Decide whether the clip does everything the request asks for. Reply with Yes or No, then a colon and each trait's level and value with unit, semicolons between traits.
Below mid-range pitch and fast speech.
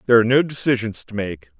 Yes: low, 115 Hz; fast, 225 wpm